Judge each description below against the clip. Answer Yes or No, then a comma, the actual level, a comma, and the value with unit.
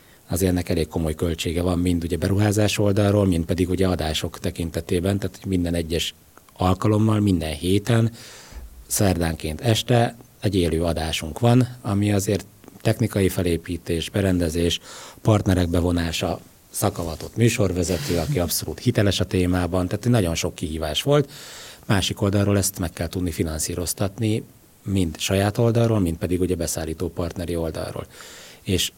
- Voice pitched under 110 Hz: Yes, very low, 90 Hz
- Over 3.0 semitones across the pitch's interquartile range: Yes, average, 3.4 semitones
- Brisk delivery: No, average, 130 wpm